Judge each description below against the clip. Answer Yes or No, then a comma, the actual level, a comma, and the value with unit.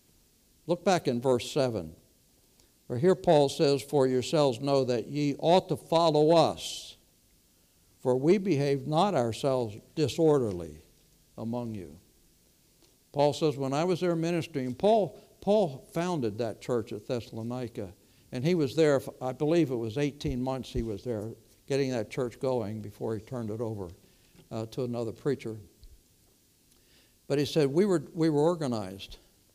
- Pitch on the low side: Yes, low, 130 Hz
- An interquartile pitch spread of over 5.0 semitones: Yes, wide, 5.4 semitones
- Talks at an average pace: Yes, average, 150 wpm